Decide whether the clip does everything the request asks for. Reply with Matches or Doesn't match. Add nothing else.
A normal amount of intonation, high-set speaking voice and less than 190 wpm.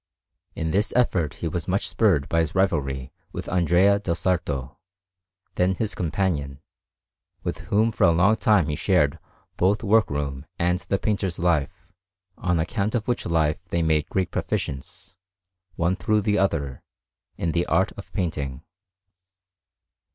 Doesn't match